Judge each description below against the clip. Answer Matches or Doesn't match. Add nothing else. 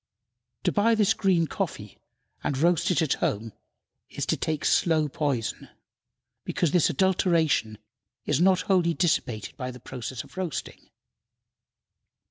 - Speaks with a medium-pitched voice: Matches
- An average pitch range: Doesn't match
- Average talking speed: Doesn't match